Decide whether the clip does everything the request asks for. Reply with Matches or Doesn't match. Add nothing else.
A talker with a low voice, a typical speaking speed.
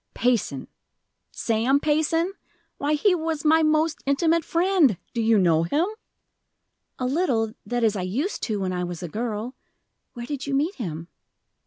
Doesn't match